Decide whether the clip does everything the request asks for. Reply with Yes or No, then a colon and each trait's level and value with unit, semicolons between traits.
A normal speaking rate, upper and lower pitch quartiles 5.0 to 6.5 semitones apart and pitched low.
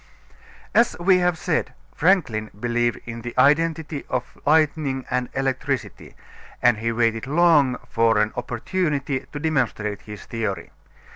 No: slow, 130 wpm; average, 5.3 semitones; low, 130 Hz